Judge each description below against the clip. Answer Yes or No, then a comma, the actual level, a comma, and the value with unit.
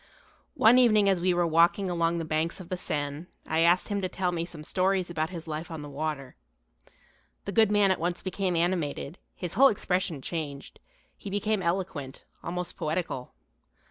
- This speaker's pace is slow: No, average, 180 wpm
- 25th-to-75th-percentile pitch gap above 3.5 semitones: No, average, 3.1 semitones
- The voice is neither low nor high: Yes, medium, 175 Hz